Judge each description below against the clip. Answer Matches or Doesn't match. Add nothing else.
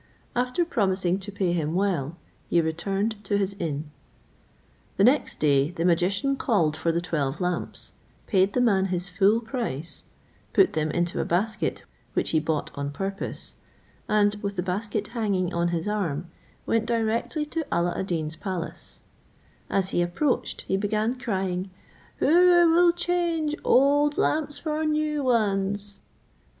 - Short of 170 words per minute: Matches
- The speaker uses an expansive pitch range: Matches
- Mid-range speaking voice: Doesn't match